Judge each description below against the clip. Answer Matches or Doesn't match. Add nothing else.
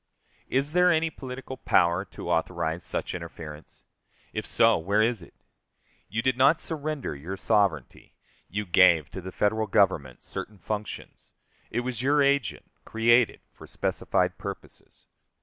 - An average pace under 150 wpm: Matches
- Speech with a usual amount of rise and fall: Doesn't match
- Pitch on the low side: Matches